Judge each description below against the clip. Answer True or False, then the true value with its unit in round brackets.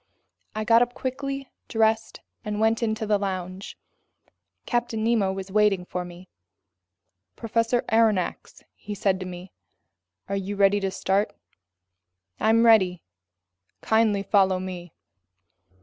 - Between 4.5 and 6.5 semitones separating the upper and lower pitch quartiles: False (3.0 semitones)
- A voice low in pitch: False (205 Hz)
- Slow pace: True (120 wpm)